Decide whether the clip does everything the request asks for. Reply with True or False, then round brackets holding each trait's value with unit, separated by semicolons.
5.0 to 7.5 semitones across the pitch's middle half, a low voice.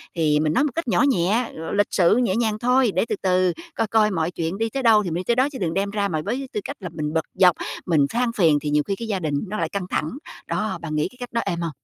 False (5.6 semitones; 195 Hz)